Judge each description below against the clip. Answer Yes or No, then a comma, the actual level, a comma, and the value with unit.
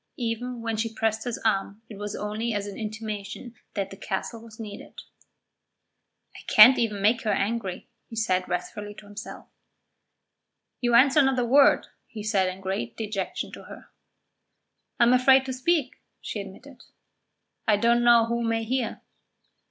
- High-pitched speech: Yes, high, 225 Hz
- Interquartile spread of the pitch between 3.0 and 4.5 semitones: No, narrow, 2.6 semitones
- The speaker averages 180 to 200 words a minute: No, average, 160 wpm